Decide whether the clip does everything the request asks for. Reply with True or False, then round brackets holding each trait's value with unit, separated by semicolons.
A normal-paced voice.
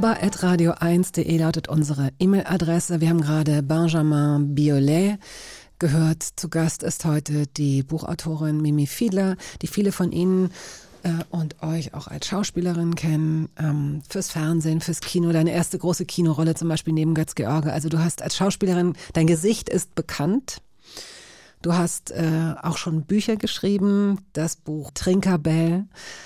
True (135 wpm)